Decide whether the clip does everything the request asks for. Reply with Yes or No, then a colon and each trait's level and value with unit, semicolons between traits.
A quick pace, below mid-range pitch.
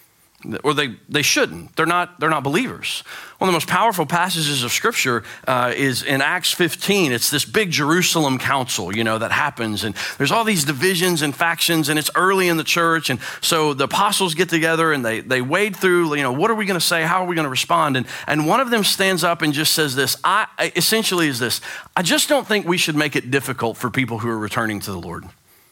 No: fast, 235 wpm; medium, 155 Hz